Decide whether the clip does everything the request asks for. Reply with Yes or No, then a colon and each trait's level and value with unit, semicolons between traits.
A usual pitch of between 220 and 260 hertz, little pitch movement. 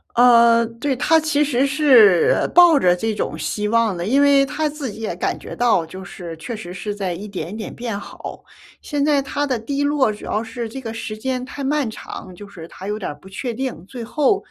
No: high, 230 Hz; average, 5.2 semitones